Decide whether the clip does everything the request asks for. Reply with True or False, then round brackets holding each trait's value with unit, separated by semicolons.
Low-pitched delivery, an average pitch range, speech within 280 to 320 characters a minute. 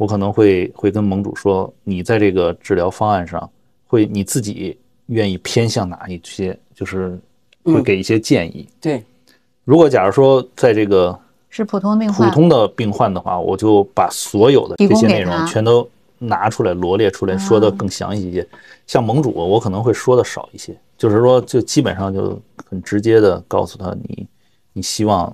False (105 Hz; 3.0 semitones; 270 characters per minute)